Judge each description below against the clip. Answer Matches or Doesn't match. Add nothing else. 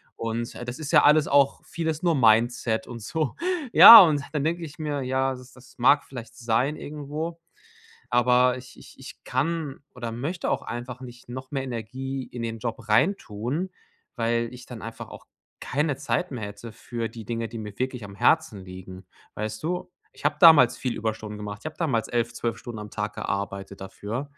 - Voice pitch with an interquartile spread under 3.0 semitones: Doesn't match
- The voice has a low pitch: Matches